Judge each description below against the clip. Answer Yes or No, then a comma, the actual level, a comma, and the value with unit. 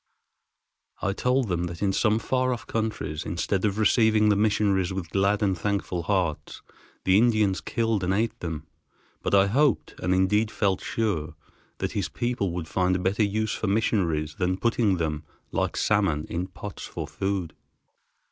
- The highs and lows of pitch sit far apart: No, average, 3.2 semitones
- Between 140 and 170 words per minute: Yes, average, 165 wpm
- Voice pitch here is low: Yes, low, 100 Hz